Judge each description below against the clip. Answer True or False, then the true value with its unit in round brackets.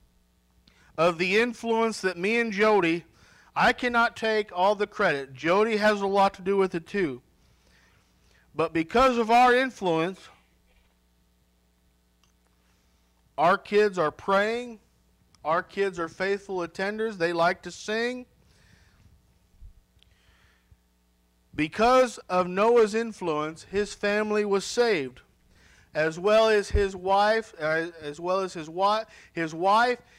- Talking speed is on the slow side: True (120 wpm)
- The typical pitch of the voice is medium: True (175 Hz)